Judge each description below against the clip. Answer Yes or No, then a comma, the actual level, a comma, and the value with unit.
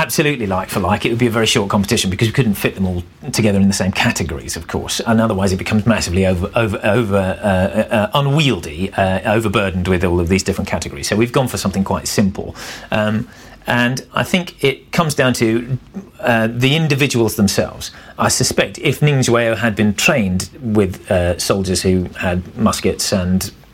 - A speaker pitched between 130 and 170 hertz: No, low, 105 Hz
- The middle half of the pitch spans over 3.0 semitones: Yes, average, 4.4 semitones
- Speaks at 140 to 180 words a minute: No, average, 190 wpm